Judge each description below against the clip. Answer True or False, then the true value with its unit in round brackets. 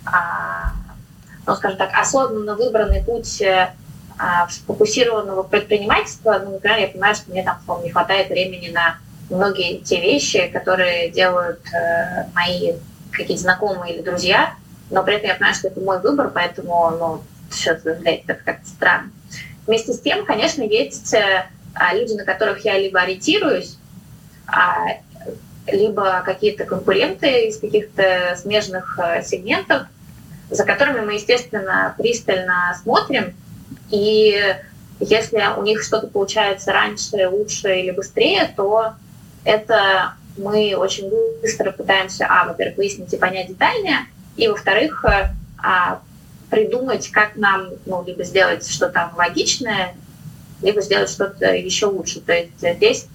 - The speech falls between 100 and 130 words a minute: True (120 wpm)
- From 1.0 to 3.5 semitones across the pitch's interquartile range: True (3.2 semitones)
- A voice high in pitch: True (195 Hz)